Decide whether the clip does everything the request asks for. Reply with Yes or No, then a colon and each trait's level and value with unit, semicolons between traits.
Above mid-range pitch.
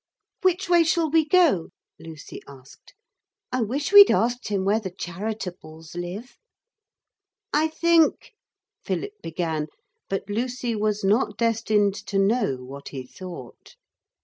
Yes: high, 210 Hz